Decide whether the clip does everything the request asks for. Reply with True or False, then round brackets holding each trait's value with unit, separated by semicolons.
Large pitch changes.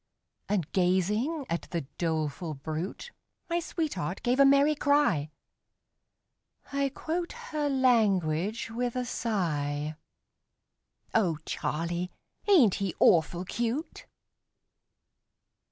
True (8.6 semitones)